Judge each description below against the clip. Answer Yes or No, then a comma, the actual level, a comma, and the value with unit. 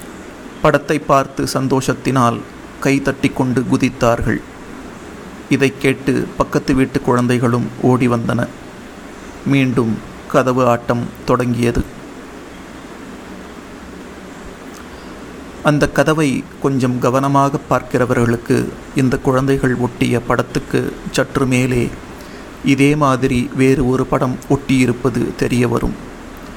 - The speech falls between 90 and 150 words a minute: No, average, 80 wpm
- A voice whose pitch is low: Yes, low, 130 Hz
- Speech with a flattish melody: Yes, narrow, 1.8 semitones